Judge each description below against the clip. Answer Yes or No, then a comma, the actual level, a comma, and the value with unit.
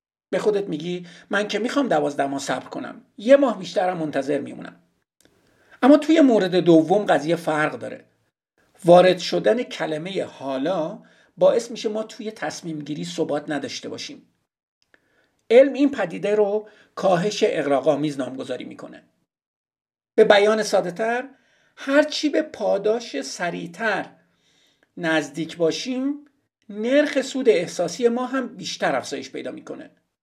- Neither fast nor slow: Yes, average, 125 wpm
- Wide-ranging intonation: Yes, wide, 7.6 semitones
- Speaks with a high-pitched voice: Yes, high, 210 Hz